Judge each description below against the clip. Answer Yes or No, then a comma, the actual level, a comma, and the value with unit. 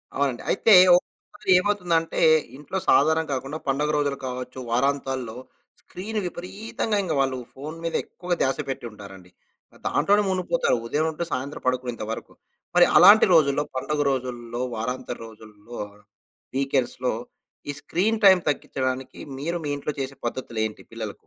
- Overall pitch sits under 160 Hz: Yes, medium, 140 Hz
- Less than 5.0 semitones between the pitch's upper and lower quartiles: No, average, 5.3 semitones